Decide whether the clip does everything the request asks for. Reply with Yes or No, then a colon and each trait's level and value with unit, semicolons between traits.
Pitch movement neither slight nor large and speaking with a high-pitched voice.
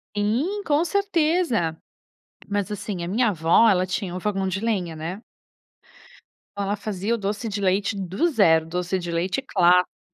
Yes: average, 4.1 semitones; high, 200 Hz